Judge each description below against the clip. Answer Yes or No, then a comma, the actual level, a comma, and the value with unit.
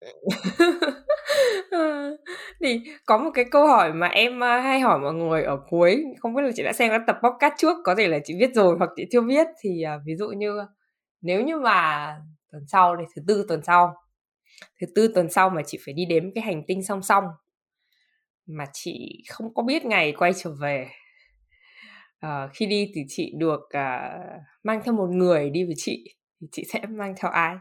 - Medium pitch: No, high, 195 Hz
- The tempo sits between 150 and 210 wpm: Yes, average, 200 wpm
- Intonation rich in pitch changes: Yes, wide, 6.8 semitones